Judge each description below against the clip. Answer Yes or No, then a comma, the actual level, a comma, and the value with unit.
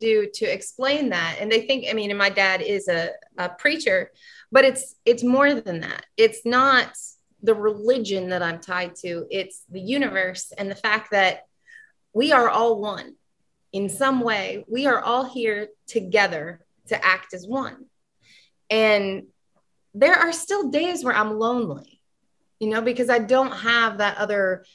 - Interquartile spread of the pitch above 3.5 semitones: Yes, average, 5.3 semitones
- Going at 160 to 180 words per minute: Yes, average, 165 wpm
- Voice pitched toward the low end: No, high, 225 Hz